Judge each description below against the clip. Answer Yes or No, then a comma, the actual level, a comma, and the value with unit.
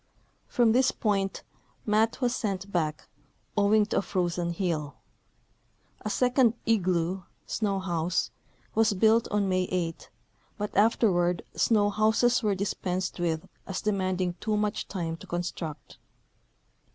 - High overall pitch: Yes, high, 195 Hz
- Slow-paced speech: Yes, slow, 130 wpm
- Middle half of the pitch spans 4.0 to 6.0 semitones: No, average, 3.4 semitones